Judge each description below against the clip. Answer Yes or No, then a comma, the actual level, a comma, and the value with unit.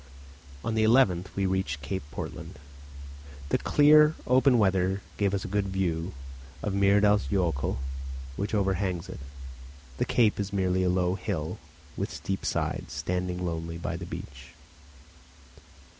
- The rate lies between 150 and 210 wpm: No, average, 140 wpm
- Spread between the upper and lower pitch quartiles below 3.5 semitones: Yes, narrow, 2.4 semitones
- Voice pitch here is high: No, very low, 95 Hz